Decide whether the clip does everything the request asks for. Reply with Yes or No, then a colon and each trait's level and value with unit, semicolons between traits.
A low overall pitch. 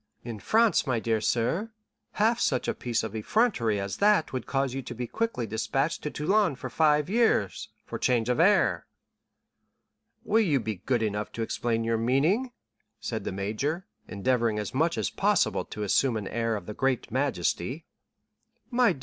Yes: low, 125 Hz